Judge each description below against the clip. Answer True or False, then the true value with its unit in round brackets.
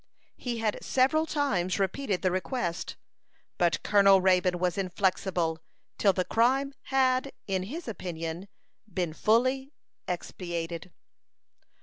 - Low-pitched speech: False (190 Hz)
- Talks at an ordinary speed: False (110 wpm)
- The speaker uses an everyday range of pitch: False (6.2 semitones)